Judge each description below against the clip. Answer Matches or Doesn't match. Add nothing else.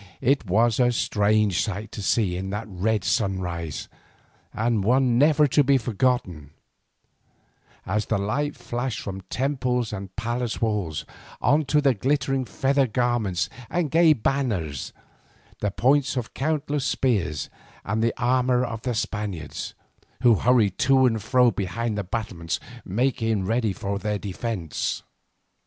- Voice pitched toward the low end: Matches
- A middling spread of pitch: Matches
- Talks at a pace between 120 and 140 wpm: Matches